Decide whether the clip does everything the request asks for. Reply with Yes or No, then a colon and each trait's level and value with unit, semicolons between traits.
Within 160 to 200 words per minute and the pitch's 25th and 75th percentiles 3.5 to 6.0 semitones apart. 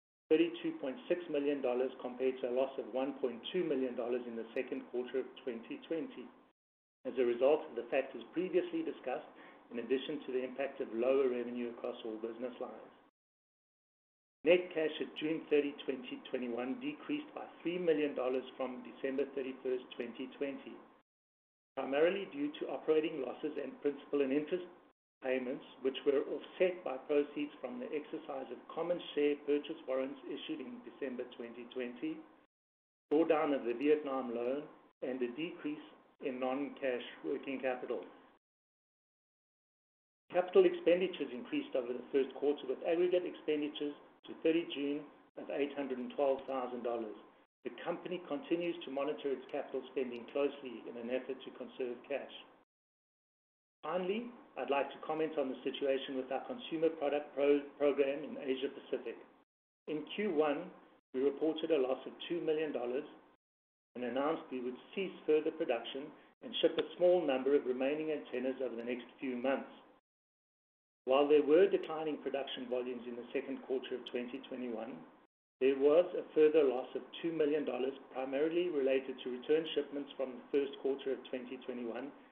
No: average, 145 wpm; average, 3.9 semitones